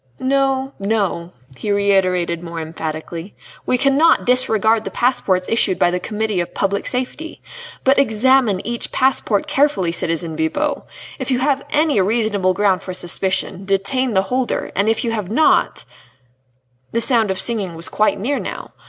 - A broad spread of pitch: Yes, wide, 5.7 semitones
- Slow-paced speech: No, average, 160 wpm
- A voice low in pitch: No, high, 210 Hz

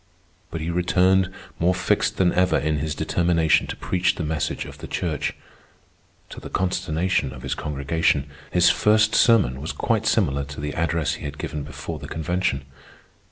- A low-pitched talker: Yes, very low, 80 Hz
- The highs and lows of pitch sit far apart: No, average, 3.7 semitones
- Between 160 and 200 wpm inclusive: Yes, average, 170 wpm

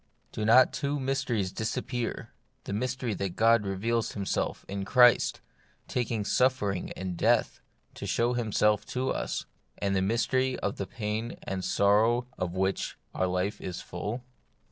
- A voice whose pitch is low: Yes, low, 110 Hz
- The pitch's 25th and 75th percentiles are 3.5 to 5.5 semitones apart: Yes, average, 4.0 semitones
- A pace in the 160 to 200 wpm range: No, average, 145 wpm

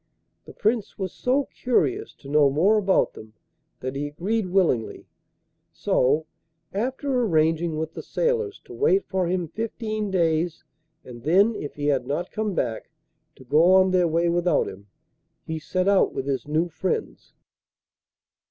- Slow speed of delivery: No, average, 155 wpm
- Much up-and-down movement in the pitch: Yes, wide, 6.1 semitones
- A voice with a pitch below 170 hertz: No, medium, 175 Hz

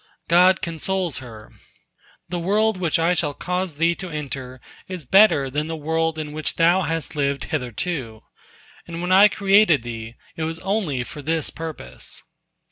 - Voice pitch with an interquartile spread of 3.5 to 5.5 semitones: Yes, average, 4.1 semitones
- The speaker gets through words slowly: No, average, 160 wpm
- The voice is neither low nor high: Yes, medium, 165 Hz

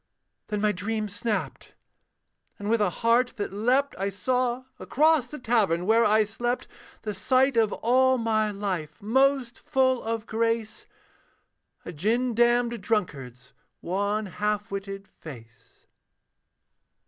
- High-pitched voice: Yes, high, 220 Hz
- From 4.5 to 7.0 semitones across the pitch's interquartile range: No, average, 3.3 semitones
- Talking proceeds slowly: Yes, slow, 125 wpm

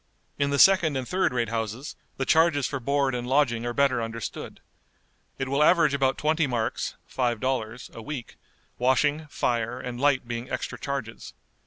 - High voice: No, low, 130 Hz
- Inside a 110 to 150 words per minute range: No, average, 170 wpm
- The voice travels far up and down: No, average, 3.2 semitones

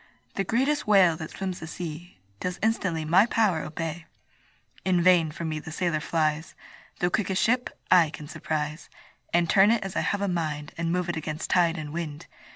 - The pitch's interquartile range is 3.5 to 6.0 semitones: No, average, 3.1 semitones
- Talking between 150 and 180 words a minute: No, average, 190 wpm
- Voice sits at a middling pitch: Yes, medium, 170 Hz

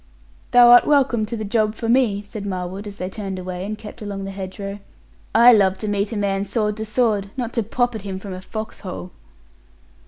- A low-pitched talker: No, high, 205 Hz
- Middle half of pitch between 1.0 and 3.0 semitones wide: Yes, narrow, 2.5 semitones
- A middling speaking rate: No, fast, 220 wpm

